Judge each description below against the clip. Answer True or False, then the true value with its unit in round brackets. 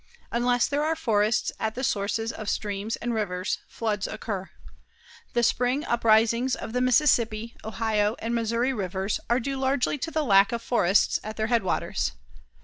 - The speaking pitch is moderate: False (230 Hz)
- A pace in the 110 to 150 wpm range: False (160 wpm)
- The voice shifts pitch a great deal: False (2.8 semitones)